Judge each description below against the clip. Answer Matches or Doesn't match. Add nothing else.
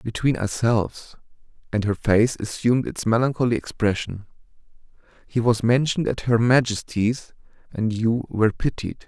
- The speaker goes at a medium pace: Doesn't match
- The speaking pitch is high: Doesn't match